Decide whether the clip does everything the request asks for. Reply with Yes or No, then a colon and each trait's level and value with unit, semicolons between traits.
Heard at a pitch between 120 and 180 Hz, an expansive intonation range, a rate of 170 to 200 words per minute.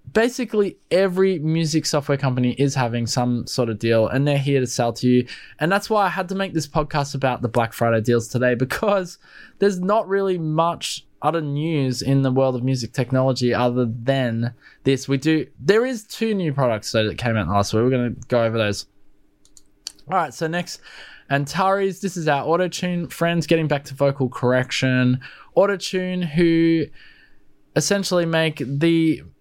Yes: medium, 140 Hz; wide, 5.9 semitones; average, 180 wpm